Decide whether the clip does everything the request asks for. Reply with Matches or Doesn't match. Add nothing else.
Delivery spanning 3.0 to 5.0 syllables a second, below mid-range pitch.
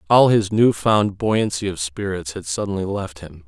Matches